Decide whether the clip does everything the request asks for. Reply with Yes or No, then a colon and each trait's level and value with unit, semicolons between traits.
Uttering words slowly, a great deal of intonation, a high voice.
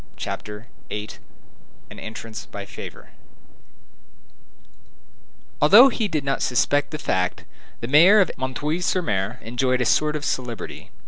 No: slow, 125 wpm; wide, 5.7 semitones; low, 130 Hz